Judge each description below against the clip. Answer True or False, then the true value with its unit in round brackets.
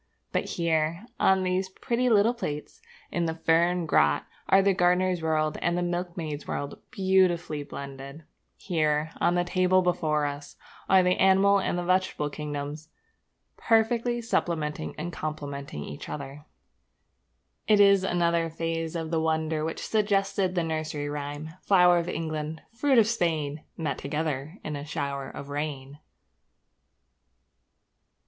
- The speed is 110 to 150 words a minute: True (140 wpm)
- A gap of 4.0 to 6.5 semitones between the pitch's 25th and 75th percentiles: False (3.6 semitones)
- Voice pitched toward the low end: False (165 Hz)